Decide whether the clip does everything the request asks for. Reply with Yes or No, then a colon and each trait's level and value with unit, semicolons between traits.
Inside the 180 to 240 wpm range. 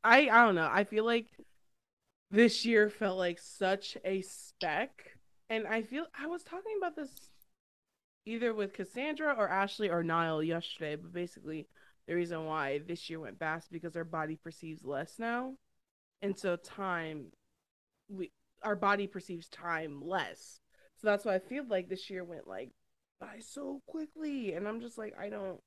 No: average, 170 wpm